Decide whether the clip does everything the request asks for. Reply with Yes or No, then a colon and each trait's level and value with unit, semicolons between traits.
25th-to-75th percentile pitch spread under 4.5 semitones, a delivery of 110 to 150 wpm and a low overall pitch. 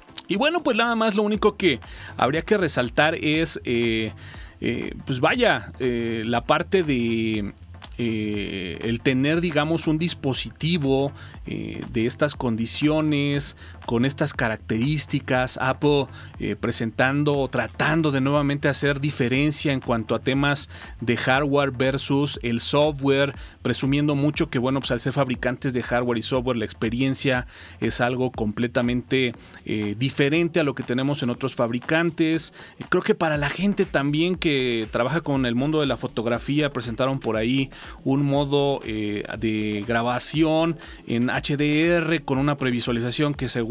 Yes: average, 4.0 semitones; average, 145 wpm; low, 130 Hz